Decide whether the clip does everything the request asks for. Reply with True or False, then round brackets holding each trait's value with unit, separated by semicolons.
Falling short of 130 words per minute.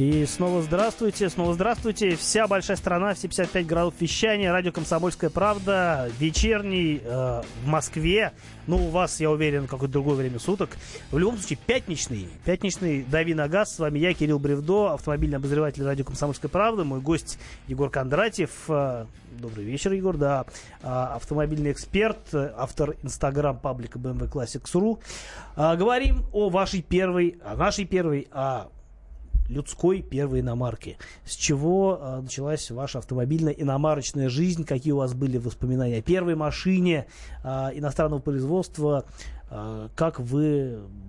False (135 wpm)